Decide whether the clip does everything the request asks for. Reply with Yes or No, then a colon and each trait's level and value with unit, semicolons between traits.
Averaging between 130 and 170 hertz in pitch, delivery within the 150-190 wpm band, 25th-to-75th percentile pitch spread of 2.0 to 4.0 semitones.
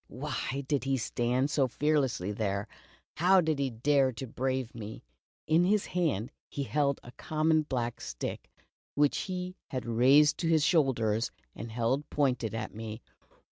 No: low, 135 Hz; average, 155 wpm; average, 4.6 semitones